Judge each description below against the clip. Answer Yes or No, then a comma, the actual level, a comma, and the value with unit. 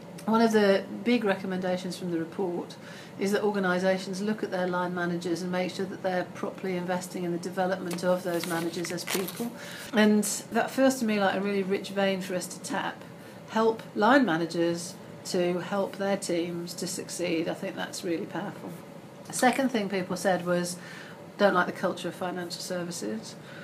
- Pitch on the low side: No, medium, 185 Hz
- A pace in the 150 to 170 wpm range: No, average, 185 wpm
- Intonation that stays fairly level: Yes, narrow, 1.9 semitones